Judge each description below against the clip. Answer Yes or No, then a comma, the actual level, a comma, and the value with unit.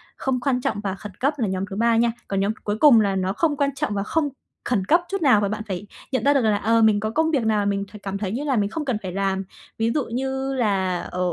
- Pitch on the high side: Yes, high, 220 Hz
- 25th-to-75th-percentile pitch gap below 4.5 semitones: No, average, 5.1 semitones